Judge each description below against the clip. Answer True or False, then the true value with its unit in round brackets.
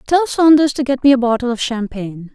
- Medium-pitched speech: False (255 Hz)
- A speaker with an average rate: False (230 wpm)